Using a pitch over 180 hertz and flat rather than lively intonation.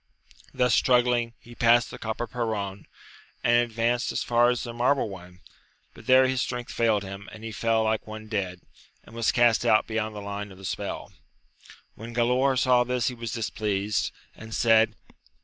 No: low, 115 Hz; narrow, 2.0 semitones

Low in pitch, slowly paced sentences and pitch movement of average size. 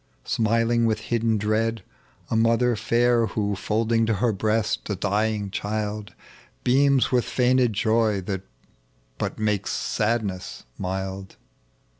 No: low, 110 Hz; slow, 125 wpm; narrow, 2.2 semitones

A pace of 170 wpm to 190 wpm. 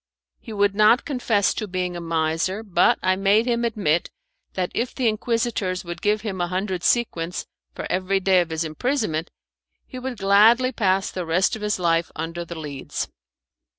Yes: average, 180 wpm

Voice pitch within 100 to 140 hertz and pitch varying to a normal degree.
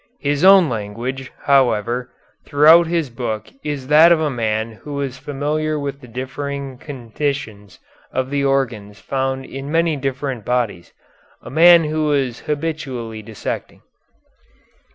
Yes: low, 135 Hz; average, 3.7 semitones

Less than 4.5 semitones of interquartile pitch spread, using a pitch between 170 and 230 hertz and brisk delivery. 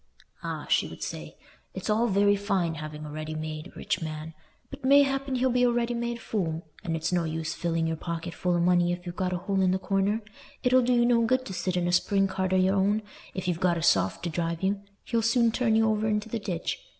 No: average, 4.8 semitones; high, 190 Hz; fast, 245 wpm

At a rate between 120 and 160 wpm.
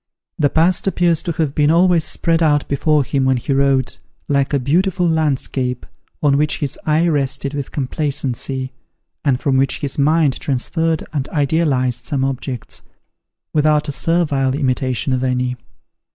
Yes: average, 150 wpm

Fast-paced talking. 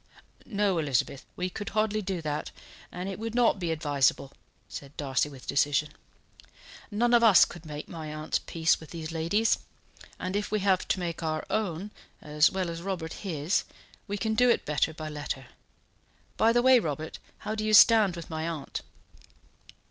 No: average, 180 wpm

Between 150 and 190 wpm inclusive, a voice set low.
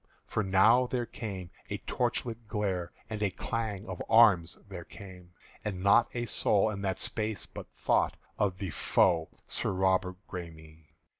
Yes: average, 155 wpm; very low, 95 Hz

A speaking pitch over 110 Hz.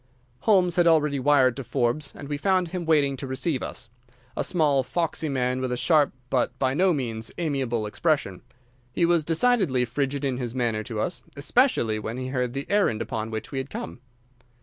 Yes: low, 135 Hz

